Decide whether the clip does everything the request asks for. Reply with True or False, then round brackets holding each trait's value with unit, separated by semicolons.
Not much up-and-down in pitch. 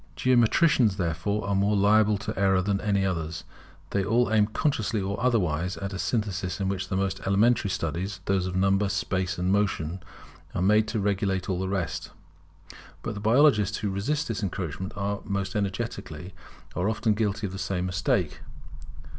True (2.2 semitones)